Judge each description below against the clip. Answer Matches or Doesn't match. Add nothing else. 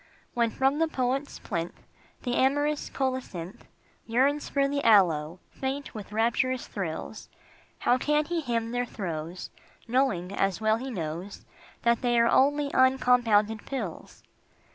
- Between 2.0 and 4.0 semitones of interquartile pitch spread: Doesn't match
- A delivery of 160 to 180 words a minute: Doesn't match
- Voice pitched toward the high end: Matches